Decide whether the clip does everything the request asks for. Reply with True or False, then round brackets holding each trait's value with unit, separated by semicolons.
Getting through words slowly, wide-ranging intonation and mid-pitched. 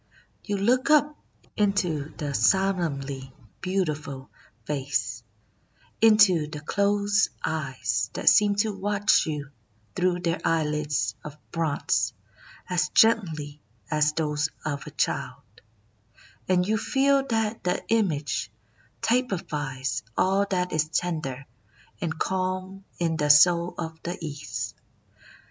False (120 wpm; 5.0 semitones; 165 Hz)